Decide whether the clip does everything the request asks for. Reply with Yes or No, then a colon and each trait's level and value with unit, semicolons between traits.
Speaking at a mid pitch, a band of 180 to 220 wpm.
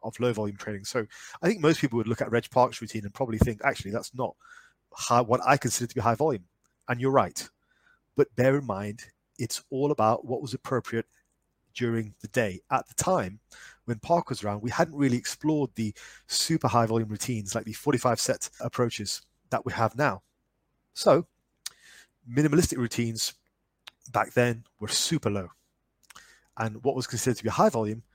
No: low, 120 Hz; average, 185 wpm